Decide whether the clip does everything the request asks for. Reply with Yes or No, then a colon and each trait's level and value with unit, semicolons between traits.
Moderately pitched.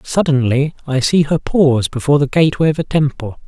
Yes: medium, 145 Hz